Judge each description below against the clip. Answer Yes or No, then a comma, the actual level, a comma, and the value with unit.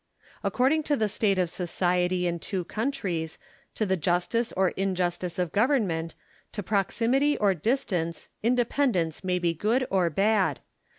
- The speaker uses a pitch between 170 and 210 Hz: Yes, high, 190 Hz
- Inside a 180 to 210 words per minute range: No, average, 140 wpm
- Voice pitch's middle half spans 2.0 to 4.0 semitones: No, average, 4.5 semitones